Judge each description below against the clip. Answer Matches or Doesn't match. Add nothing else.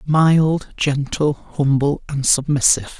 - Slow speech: Matches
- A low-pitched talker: Doesn't match